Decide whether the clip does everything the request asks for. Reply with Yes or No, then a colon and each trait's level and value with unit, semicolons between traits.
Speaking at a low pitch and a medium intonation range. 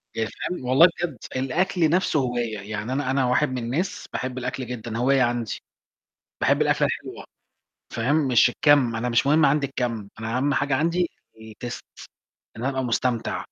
Yes: low, 130 Hz; average, 3.3 semitones